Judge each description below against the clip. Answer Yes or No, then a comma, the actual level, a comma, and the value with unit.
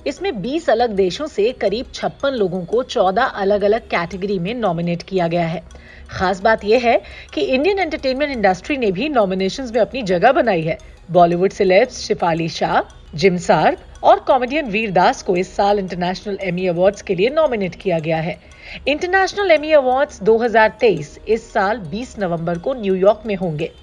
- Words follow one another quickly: No, average, 170 wpm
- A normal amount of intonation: No, wide, 6.2 semitones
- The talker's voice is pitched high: Yes, high, 205 Hz